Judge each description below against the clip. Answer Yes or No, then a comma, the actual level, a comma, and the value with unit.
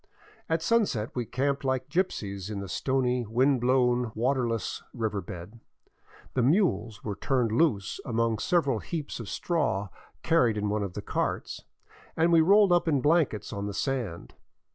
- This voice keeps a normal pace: Yes, average, 160 wpm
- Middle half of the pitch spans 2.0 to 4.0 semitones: No, wide, 5.5 semitones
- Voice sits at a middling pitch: No, low, 125 Hz